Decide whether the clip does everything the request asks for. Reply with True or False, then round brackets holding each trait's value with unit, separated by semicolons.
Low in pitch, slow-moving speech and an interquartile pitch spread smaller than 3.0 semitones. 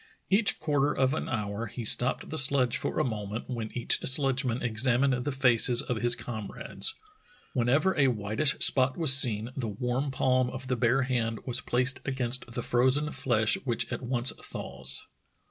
False (125 Hz; 175 wpm; 2.4 semitones)